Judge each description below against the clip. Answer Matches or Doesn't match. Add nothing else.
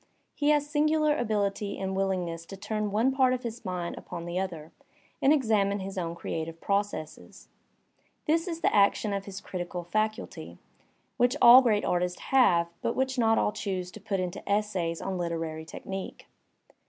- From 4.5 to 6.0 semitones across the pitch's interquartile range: Matches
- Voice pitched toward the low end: Doesn't match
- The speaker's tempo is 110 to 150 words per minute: Doesn't match